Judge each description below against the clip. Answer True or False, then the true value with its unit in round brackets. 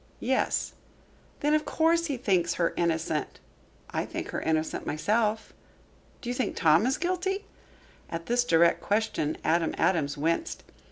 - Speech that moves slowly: False (145 wpm)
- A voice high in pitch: True (200 Hz)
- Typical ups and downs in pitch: False (8.3 semitones)